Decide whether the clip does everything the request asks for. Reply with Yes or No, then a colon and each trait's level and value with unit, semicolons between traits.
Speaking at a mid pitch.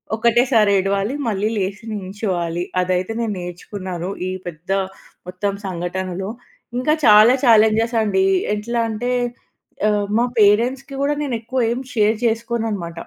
No: high, 210 Hz